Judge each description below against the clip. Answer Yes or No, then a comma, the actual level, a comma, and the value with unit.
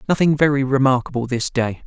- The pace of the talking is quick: No, average, 160 wpm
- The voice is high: No, low, 135 Hz